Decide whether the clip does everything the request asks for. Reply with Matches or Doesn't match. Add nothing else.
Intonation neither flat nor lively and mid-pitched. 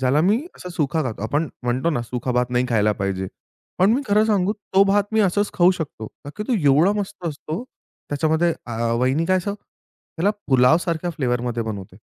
Doesn't match